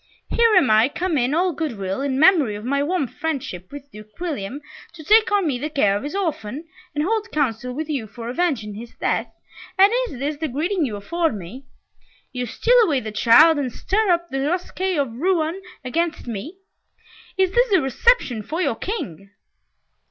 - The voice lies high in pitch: Yes, very high, 290 Hz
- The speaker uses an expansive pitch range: Yes, wide, 6.9 semitones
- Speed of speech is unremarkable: Yes, average, 190 wpm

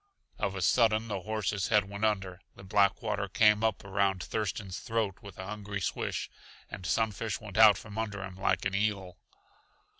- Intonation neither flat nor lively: No, narrow, 1.8 semitones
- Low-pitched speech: Yes, low, 100 Hz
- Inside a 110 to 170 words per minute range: No, average, 180 wpm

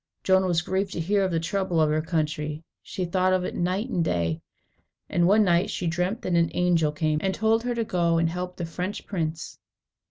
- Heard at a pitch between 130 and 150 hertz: No, medium, 175 Hz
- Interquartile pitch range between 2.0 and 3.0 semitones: Yes, narrow, 2.6 semitones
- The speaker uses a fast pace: Yes, fast, 220 wpm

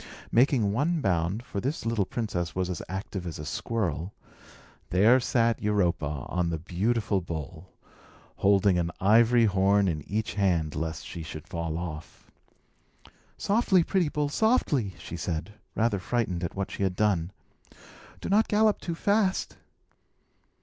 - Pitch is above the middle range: No, low, 100 Hz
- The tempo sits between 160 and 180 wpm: No, average, 145 wpm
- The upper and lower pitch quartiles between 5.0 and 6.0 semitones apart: Yes, wide, 5.6 semitones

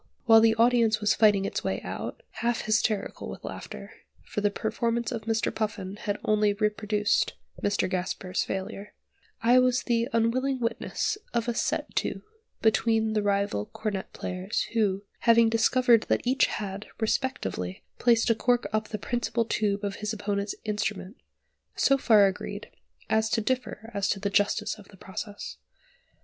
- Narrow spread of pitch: Yes, narrow, 2.2 semitones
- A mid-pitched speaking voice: No, high, 215 Hz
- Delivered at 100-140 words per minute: No, average, 160 wpm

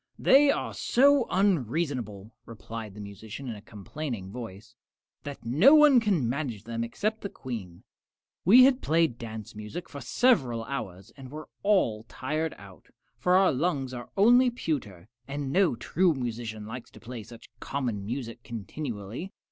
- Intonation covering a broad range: Yes, wide, 7.9 semitones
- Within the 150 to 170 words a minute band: Yes, average, 155 wpm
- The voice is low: Yes, low, 125 Hz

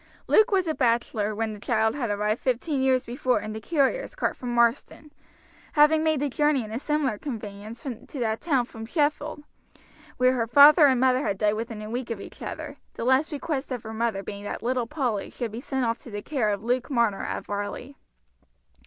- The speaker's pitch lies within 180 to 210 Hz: No, high, 245 Hz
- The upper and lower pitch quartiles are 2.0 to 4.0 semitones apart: No, average, 4.4 semitones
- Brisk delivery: Yes, fast, 210 wpm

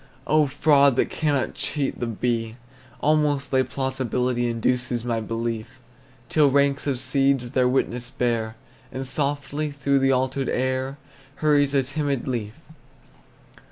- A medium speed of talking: No, slow, 130 wpm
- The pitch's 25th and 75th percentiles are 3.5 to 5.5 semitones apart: No, narrow, 2.5 semitones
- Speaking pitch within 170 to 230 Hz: No, low, 130 Hz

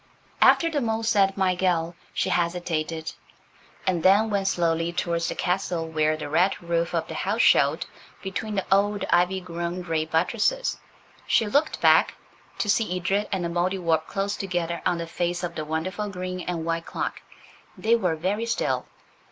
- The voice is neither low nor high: Yes, medium, 180 Hz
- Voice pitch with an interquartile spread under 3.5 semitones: Yes, average, 2.7 semitones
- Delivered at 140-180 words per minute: Yes, average, 170 wpm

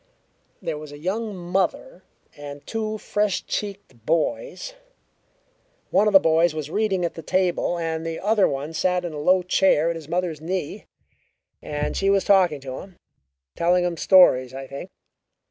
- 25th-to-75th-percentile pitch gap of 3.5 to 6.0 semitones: Yes, average, 4.0 semitones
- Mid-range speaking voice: Yes, medium, 175 Hz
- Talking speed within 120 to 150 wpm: No, average, 165 wpm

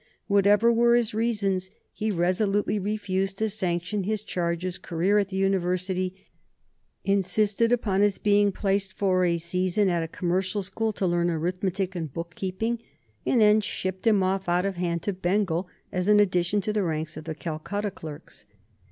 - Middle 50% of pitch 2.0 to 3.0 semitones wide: Yes, average, 2.7 semitones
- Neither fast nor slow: Yes, average, 170 wpm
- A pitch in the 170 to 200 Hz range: Yes, high, 190 Hz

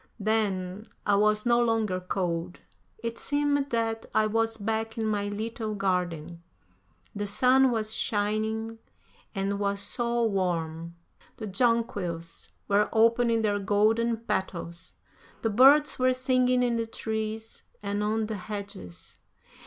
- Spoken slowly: Yes, slow, 130 wpm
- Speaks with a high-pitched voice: Yes, high, 215 Hz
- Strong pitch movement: No, narrow, 2.5 semitones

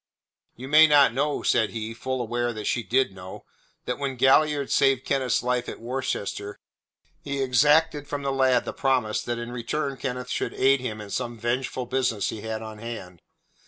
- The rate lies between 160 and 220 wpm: Yes, average, 190 wpm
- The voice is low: Yes, low, 125 Hz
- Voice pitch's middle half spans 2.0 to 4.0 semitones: Yes, average, 2.8 semitones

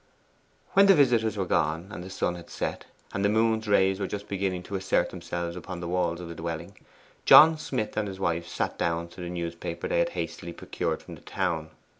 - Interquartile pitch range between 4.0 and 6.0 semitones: No, average, 3.5 semitones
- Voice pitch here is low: Yes, very low, 95 Hz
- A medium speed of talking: No, fast, 215 wpm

